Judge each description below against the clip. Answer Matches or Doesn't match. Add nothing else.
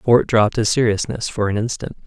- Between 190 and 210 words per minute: Matches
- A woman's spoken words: Doesn't match